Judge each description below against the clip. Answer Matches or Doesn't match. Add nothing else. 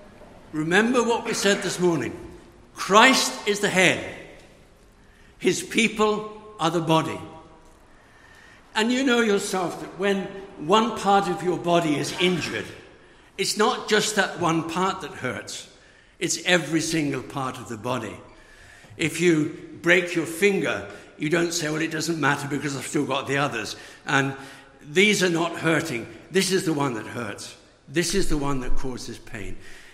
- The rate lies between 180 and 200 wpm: Doesn't match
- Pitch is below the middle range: Doesn't match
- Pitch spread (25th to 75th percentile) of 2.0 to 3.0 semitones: Doesn't match